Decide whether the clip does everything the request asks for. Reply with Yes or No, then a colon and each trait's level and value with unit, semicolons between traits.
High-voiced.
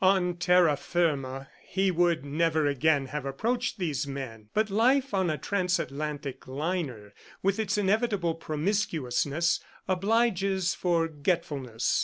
No: medium, 170 Hz